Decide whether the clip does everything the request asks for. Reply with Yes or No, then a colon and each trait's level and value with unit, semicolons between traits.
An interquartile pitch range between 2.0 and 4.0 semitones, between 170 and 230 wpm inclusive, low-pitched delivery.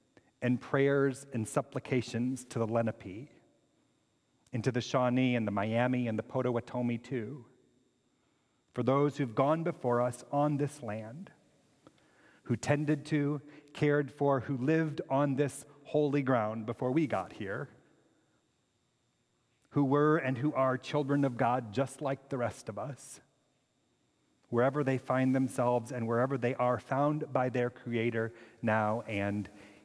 No: average, 3.2 semitones; average, 140 wpm; low, 130 Hz